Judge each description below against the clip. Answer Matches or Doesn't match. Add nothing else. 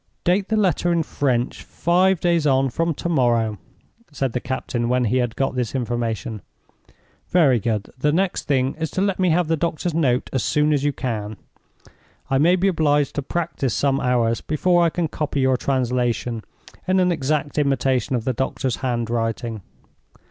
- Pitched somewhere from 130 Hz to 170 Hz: Matches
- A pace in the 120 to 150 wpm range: Doesn't match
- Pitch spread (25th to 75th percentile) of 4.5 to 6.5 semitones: Matches